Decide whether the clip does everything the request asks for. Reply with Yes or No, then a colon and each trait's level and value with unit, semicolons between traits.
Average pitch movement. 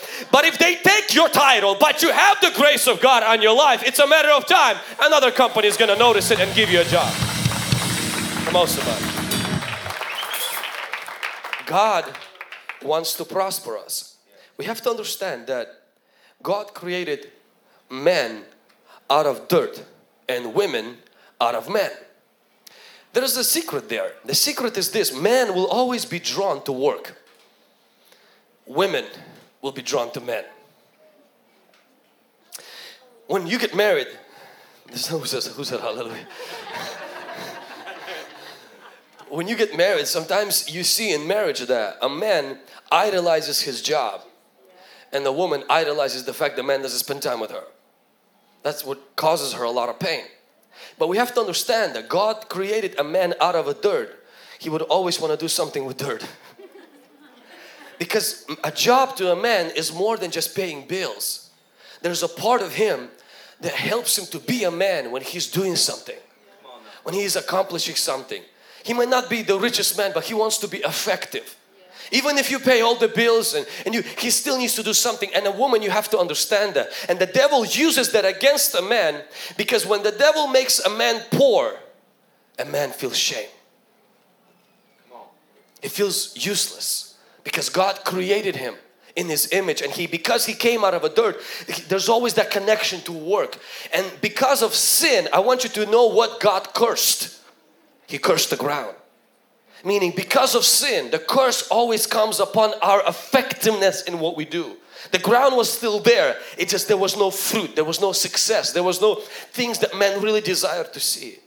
No: wide, 5.8 semitones